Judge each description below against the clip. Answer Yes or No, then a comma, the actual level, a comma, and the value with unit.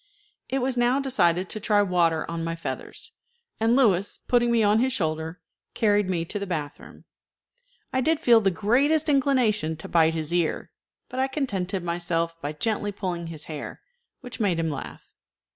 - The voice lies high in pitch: Yes, high, 200 Hz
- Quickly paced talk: No, average, 175 wpm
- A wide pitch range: Yes, wide, 6.4 semitones